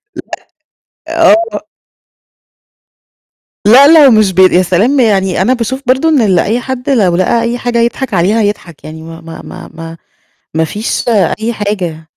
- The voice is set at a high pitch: Yes, high, 215 Hz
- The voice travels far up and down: Yes, wide, 5.7 semitones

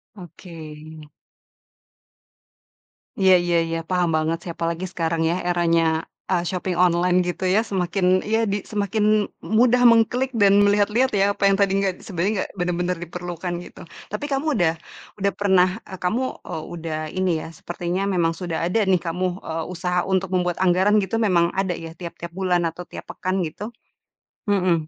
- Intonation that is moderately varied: No, narrow, 2.3 semitones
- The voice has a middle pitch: Yes, medium, 180 Hz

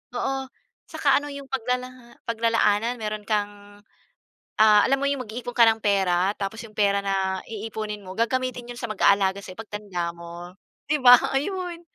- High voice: Yes, high, 215 Hz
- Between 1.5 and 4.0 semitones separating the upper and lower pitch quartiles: Yes, average, 3.6 semitones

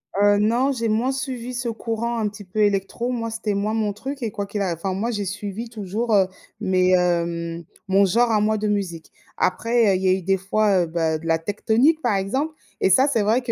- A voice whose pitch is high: Yes, high, 210 Hz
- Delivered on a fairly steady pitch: No, average, 3.4 semitones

